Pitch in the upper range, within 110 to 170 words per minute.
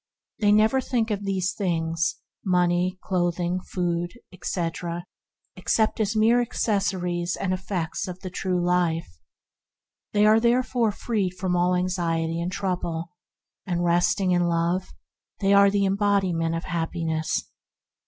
No: medium, 180 Hz; average, 140 wpm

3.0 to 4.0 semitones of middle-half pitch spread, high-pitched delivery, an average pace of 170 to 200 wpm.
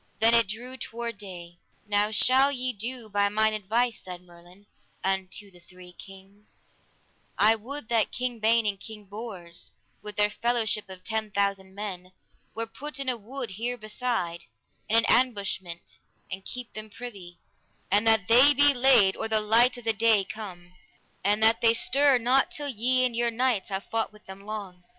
Yes: average, 3.4 semitones; high, 215 Hz; average, 180 wpm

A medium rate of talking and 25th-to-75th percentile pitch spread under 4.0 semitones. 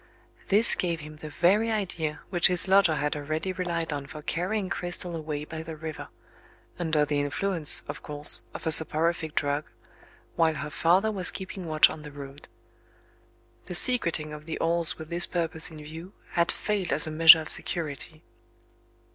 Yes: average, 170 wpm; narrow, 2.6 semitones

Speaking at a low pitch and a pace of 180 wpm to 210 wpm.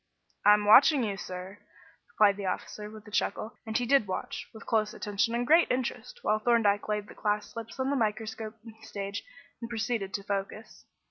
No: high, 215 Hz; average, 185 wpm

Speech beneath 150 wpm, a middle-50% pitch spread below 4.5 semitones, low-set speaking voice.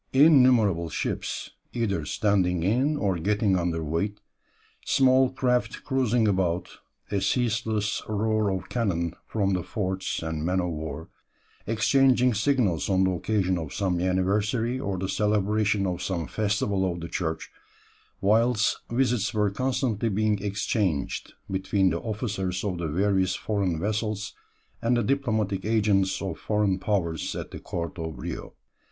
Yes: average, 140 wpm; average, 3.3 semitones; low, 100 Hz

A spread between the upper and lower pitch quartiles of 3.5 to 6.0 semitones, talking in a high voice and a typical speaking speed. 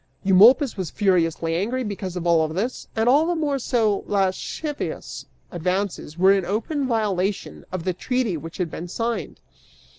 Yes: average, 4.9 semitones; high, 195 Hz; average, 160 wpm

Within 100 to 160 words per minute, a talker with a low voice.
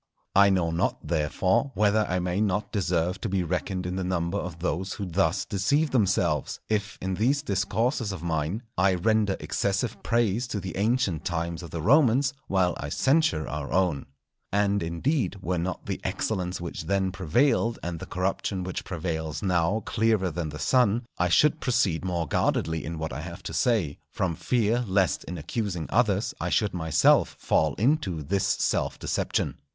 No: average, 175 wpm; very low, 95 Hz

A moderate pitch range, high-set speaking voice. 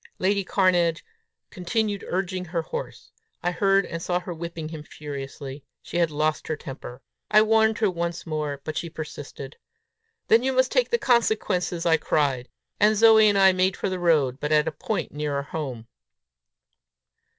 No: average, 4.7 semitones; medium, 170 Hz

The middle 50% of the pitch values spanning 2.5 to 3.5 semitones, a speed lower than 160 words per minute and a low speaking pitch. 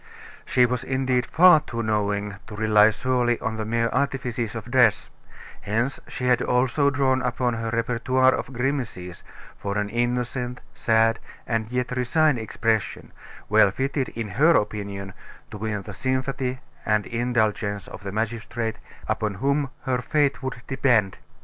Yes: average, 3.2 semitones; average, 150 wpm; low, 120 Hz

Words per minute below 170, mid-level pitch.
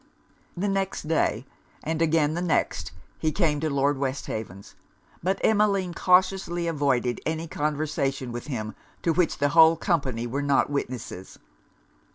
Yes: average, 140 wpm; medium, 150 Hz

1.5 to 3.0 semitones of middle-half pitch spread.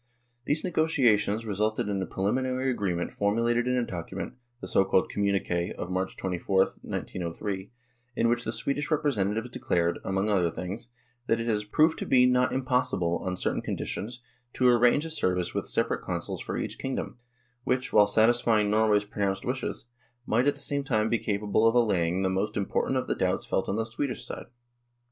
No: average, 4.4 semitones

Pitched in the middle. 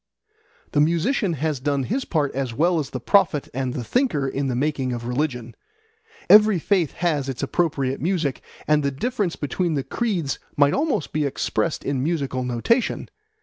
Yes: medium, 150 Hz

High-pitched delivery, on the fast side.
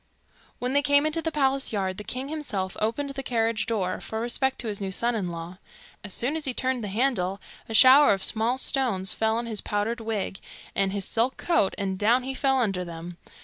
Yes: high, 225 Hz; fast, 220 wpm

